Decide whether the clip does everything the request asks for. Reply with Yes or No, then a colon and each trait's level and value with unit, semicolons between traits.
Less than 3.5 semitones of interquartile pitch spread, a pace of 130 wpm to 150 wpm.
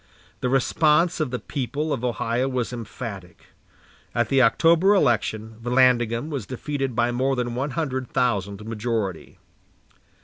Yes: average, 3.0 semitones; slow, 135 wpm